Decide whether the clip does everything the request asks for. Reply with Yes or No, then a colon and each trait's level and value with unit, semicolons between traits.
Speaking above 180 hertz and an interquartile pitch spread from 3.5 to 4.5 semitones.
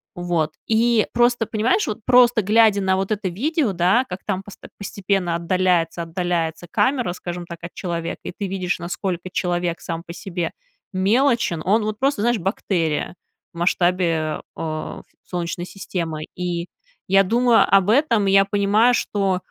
Yes: high, 190 Hz; average, 3.8 semitones